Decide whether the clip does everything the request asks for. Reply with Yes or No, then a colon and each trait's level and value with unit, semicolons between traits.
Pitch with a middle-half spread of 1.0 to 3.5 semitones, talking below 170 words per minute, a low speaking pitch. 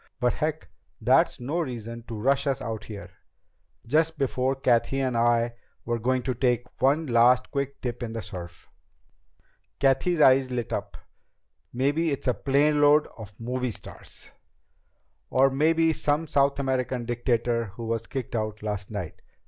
Yes: average, 3.0 semitones; average, 150 wpm; low, 125 Hz